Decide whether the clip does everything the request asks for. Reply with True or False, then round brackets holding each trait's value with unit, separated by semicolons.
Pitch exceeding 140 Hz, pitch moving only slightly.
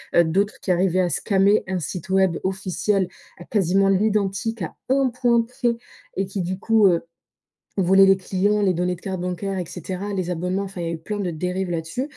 True (190 Hz; 2.1 semitones)